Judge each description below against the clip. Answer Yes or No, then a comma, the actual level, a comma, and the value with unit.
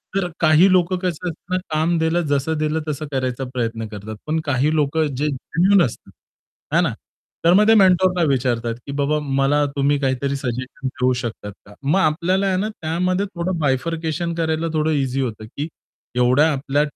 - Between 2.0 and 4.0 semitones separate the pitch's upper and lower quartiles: No, average, 4.4 semitones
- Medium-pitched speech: Yes, medium, 150 Hz